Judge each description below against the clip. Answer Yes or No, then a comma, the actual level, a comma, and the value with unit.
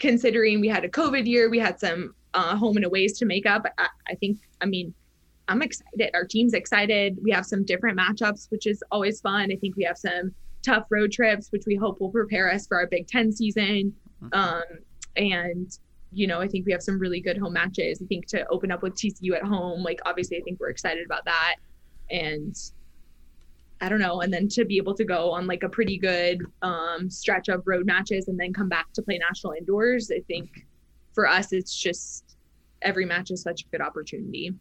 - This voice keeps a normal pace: No, fast, 220 wpm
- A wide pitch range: No, average, 3.0 semitones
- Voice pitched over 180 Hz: Yes, high, 190 Hz